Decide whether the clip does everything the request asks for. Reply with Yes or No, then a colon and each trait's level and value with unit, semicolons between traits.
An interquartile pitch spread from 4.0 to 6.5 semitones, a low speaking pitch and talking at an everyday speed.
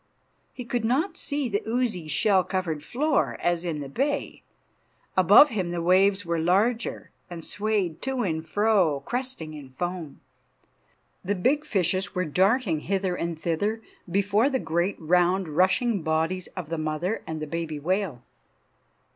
No: average, 5.1 semitones; medium, 185 Hz; average, 150 wpm